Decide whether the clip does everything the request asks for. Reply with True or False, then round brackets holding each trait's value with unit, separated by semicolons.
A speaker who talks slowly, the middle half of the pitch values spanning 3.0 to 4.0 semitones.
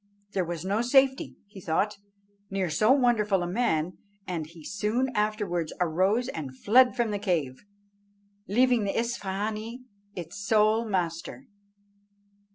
False (130 wpm; 4.8 semitones)